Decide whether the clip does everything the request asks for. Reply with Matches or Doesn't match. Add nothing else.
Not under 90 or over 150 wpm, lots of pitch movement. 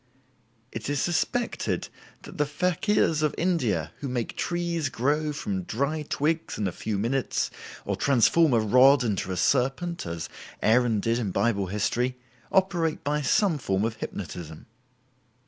Matches